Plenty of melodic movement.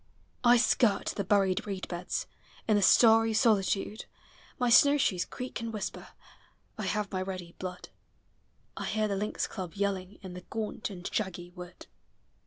No: average, 3.1 semitones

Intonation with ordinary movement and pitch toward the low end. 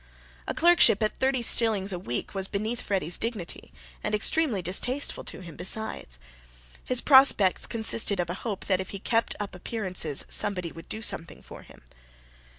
No: average, 4.1 semitones; high, 205 Hz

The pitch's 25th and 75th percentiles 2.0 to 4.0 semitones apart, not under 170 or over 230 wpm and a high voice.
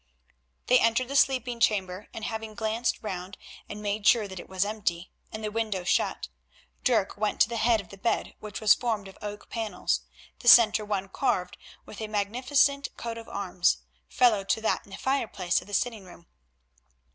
Yes: average, 2.9 semitones; average, 190 wpm; high, 215 Hz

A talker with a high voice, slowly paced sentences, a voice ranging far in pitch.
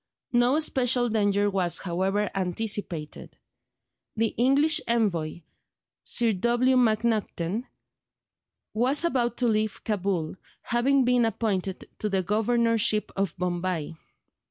No: high, 215 Hz; slow, 105 wpm; average, 3.9 semitones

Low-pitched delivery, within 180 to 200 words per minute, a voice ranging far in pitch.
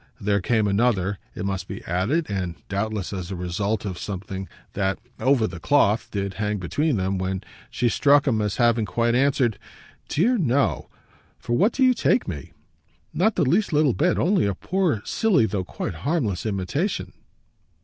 No: low, 110 Hz; average, 170 wpm; wide, 6.8 semitones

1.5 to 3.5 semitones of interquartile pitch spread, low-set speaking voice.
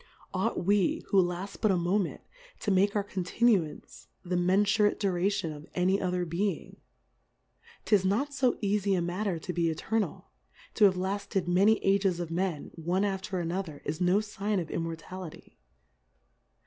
No: narrow, 2.6 semitones; high, 190 Hz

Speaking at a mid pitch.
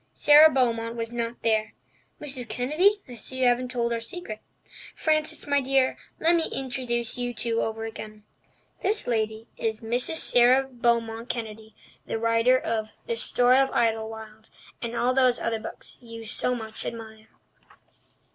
No: high, 235 Hz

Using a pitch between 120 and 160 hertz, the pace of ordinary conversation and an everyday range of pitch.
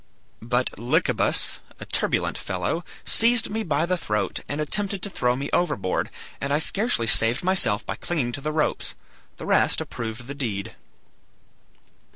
No: medium, 140 Hz; average, 155 wpm; wide, 7.4 semitones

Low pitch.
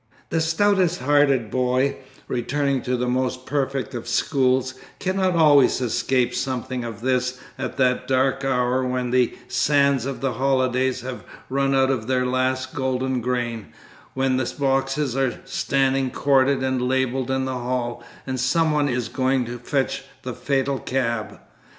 Yes: low, 130 Hz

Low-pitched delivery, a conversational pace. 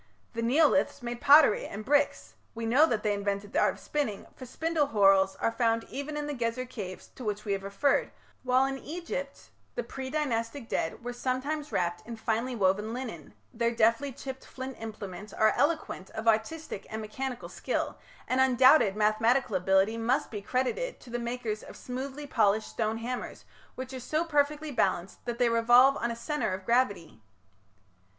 No: high, 240 Hz; average, 180 wpm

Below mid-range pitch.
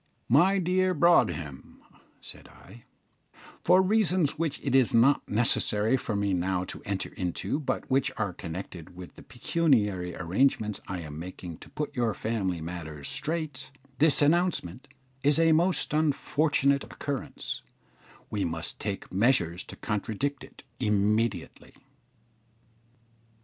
Yes: low, 115 Hz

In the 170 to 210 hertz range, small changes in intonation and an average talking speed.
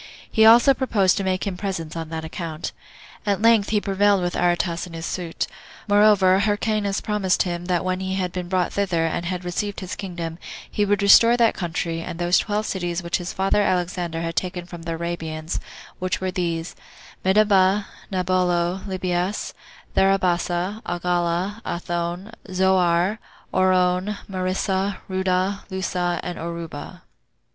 Yes: medium, 185 Hz; narrow, 2.3 semitones; average, 150 wpm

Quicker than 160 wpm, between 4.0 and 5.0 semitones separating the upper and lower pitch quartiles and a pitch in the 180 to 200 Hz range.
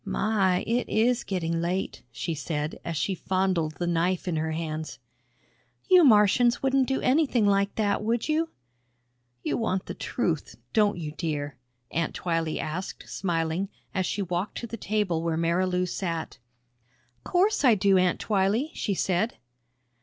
No: average, 155 wpm; average, 4.6 semitones; medium, 185 Hz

